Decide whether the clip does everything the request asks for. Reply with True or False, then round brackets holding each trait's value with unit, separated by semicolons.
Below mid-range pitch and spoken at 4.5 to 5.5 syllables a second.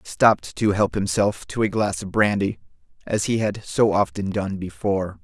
True (100 Hz; 5.0 syllables/s)